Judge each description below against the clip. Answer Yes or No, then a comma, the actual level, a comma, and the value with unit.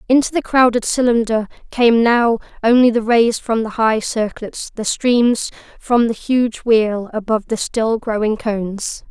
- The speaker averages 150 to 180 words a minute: Yes, average, 160 wpm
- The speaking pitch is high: Yes, high, 230 Hz